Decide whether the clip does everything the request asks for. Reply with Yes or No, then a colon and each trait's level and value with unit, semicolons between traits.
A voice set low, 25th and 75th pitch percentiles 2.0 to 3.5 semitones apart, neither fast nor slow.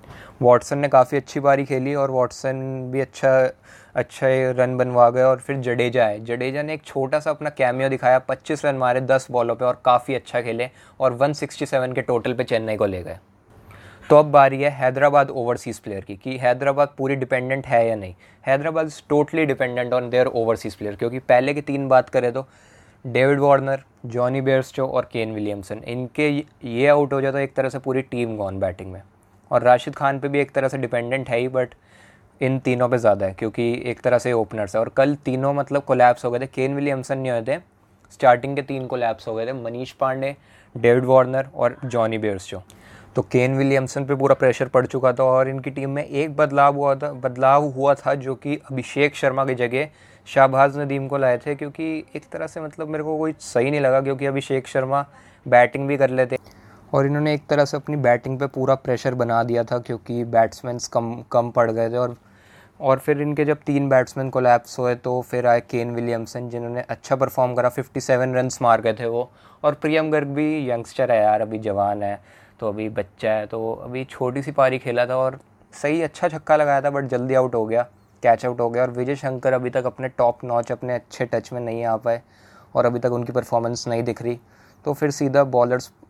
No: low, 130 Hz; average, 2.7 semitones; fast, 210 wpm